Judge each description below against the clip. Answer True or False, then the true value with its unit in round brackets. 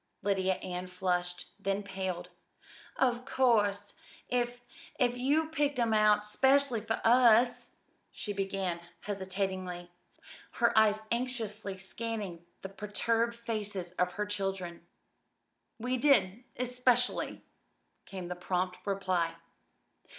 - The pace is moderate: False (110 wpm)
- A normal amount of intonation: True (4.2 semitones)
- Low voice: False (210 Hz)